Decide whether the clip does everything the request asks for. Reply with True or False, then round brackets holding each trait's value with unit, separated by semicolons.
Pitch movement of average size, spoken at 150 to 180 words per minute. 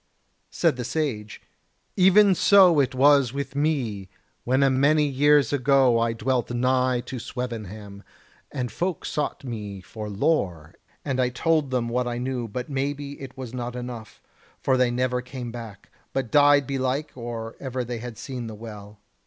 True (3.1 semitones; 170 wpm)